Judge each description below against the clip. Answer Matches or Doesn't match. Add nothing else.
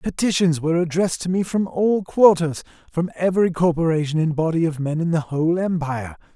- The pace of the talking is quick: Doesn't match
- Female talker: Doesn't match